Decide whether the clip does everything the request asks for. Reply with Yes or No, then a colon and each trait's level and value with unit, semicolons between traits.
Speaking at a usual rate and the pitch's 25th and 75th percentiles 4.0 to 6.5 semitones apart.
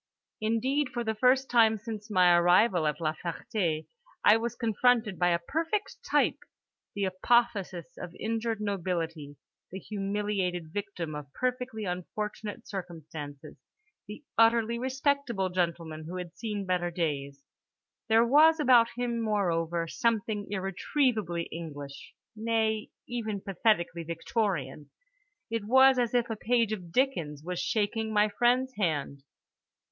No: slow, 125 wpm; average, 5.2 semitones